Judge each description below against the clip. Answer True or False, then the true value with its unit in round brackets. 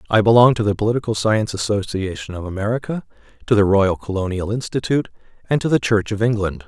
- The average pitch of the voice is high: False (105 Hz)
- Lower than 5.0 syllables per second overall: False (6.5 syllables/s)